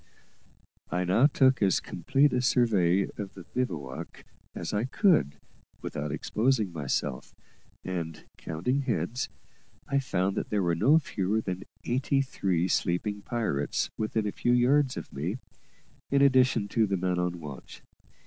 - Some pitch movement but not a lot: No, wide, 6.6 semitones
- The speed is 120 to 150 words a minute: Yes, average, 145 wpm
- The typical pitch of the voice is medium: No, low, 105 Hz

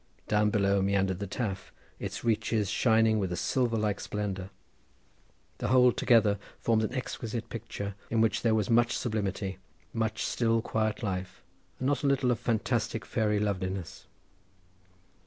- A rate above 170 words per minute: No, average, 150 wpm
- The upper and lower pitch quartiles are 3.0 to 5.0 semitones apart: No, narrow, 2.6 semitones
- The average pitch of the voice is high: No, low, 110 Hz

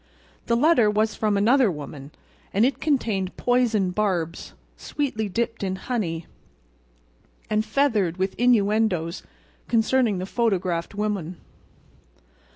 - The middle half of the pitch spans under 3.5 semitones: No, average, 4.2 semitones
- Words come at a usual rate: No, slow, 110 wpm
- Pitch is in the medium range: No, high, 210 Hz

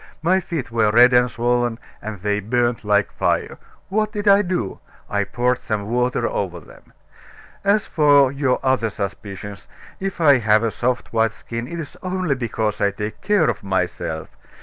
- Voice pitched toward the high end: No, low, 120 Hz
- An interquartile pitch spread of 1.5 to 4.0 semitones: No, wide, 5.6 semitones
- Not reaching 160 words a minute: No, average, 170 wpm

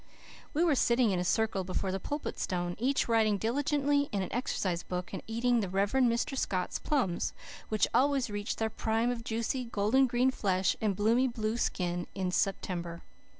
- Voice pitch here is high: Yes, high, 220 Hz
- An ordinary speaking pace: Yes, average, 180 wpm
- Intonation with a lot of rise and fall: No, average, 4.7 semitones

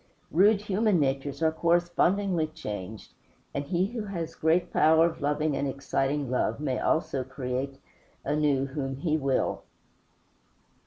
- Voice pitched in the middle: Yes, medium, 150 Hz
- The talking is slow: Yes, slow, 130 wpm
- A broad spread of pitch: No, average, 4.1 semitones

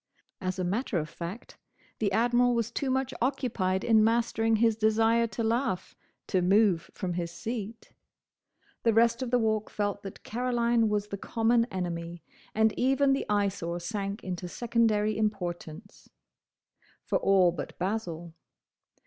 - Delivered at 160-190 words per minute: No, average, 145 wpm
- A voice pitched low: No, high, 215 Hz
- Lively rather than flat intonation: No, average, 3.8 semitones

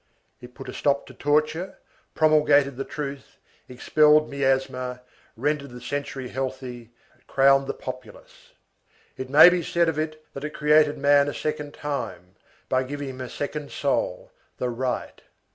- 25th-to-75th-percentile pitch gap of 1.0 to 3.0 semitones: Yes, narrow, 2.6 semitones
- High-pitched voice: No, medium, 140 Hz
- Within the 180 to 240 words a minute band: No, average, 150 wpm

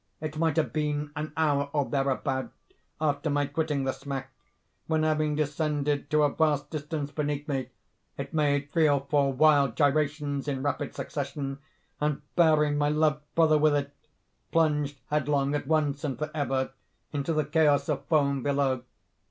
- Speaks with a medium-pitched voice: Yes, medium, 145 Hz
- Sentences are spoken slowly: No, average, 160 wpm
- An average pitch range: No, narrow, 1.5 semitones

